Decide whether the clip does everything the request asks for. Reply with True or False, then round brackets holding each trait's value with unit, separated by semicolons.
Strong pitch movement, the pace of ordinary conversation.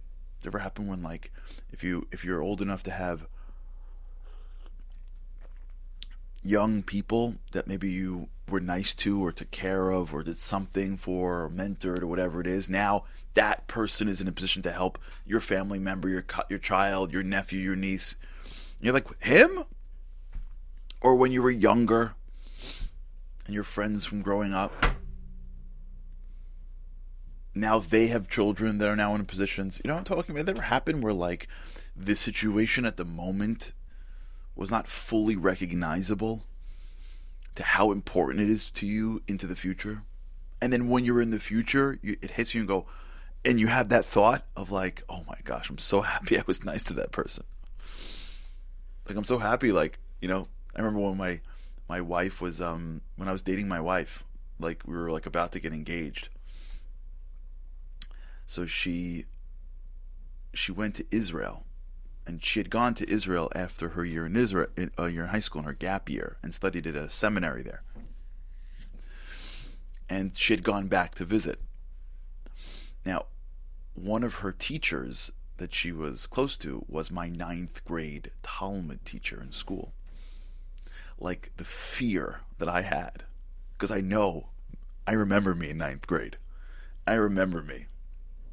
True (8.0 semitones; 165 wpm)